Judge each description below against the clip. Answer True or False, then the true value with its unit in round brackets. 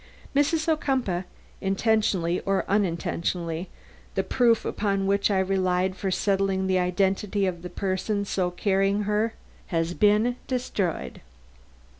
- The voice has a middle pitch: False (195 Hz)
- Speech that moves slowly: True (120 wpm)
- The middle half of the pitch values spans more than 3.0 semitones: False (2.4 semitones)